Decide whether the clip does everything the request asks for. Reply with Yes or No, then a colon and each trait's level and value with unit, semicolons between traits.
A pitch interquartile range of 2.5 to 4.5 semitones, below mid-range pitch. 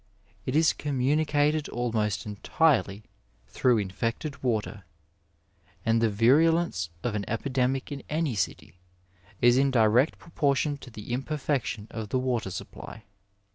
No: average, 4.9 semitones; low, 125 Hz